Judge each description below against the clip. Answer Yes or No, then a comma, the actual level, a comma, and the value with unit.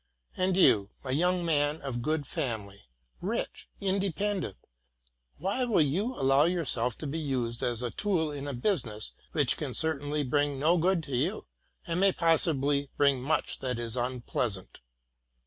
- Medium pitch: Yes, medium, 145 Hz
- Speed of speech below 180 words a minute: Yes, average, 155 wpm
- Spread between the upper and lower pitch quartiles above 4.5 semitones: Yes, wide, 5.4 semitones